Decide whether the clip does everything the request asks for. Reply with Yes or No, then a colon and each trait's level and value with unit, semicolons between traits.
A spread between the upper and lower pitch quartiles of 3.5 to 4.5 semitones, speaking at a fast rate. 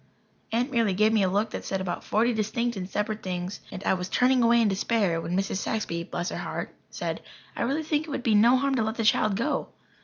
Yes: average, 3.8 semitones; fast, 245 wpm